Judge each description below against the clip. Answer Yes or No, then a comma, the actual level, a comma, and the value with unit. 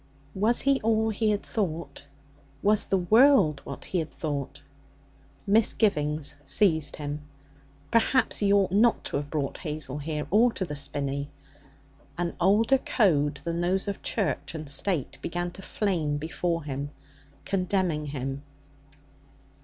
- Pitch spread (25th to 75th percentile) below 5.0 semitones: No, wide, 5.6 semitones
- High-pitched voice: No, medium, 170 Hz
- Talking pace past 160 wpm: No, average, 140 wpm